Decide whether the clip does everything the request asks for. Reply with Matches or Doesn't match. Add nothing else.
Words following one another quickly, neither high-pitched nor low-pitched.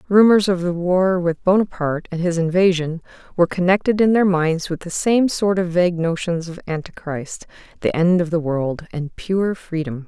Doesn't match